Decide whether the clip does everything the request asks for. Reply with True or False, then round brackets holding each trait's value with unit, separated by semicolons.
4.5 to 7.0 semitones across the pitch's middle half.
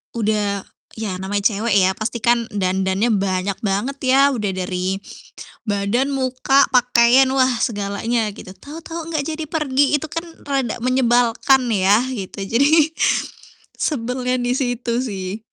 True (4.8 semitones)